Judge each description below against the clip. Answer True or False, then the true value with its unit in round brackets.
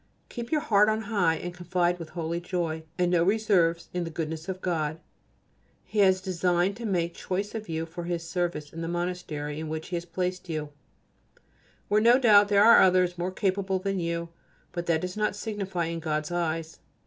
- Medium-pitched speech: True (175 Hz)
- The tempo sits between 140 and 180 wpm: False (195 wpm)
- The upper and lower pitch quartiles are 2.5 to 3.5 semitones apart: True (2.9 semitones)